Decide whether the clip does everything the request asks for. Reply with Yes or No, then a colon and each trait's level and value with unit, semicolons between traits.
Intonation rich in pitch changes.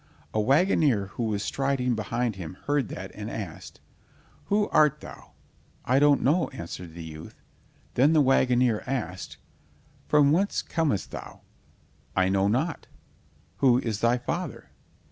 Yes: wide, 6.1 semitones